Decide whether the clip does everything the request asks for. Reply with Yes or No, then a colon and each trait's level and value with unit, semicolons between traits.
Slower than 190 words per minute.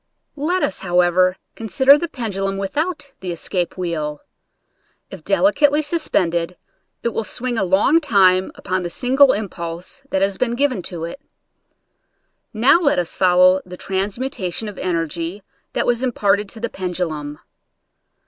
Yes: average, 150 wpm